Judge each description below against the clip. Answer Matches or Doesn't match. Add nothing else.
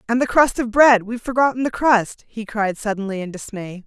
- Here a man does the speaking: Doesn't match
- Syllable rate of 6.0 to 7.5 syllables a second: Doesn't match